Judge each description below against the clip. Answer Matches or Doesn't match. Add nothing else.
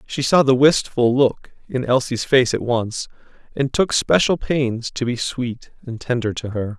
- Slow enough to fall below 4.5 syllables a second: Matches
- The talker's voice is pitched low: Matches